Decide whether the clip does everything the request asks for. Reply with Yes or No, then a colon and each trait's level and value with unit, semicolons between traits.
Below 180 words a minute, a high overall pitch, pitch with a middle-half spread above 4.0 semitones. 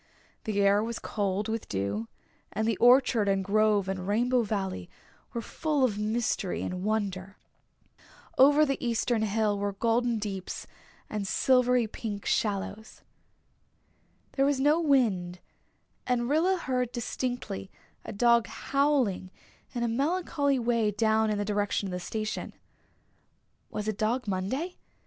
No: slow, 135 wpm; high, 220 Hz; average, 3.7 semitones